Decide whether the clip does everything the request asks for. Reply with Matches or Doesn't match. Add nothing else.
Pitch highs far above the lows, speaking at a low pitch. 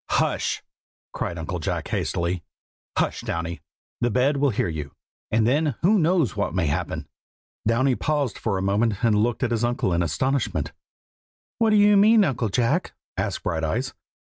Matches